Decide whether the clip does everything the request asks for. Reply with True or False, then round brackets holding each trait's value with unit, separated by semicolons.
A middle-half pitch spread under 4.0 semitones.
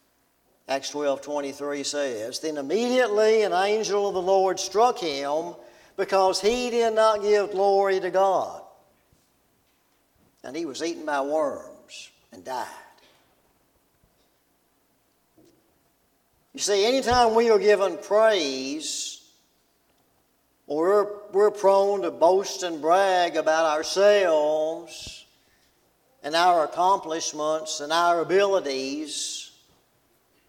False (5.2 semitones)